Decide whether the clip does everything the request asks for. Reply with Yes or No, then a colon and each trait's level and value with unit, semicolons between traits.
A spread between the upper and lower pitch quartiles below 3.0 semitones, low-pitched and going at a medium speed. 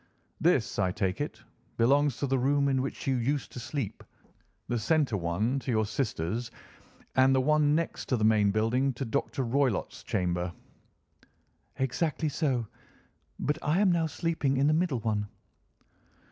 No: average, 4.7 semitones; low, 130 Hz; average, 160 wpm